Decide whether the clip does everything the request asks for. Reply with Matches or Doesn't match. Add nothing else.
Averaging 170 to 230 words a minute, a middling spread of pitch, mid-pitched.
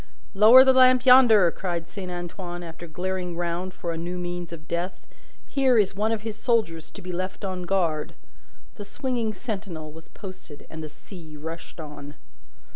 Matches